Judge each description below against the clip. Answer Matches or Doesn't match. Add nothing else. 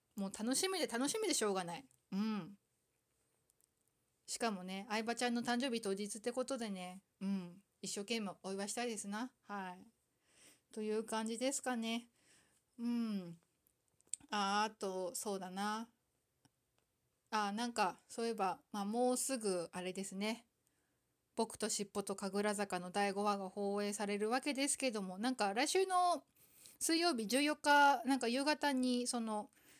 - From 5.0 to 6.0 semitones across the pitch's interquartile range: Doesn't match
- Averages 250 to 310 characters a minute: Matches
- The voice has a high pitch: Matches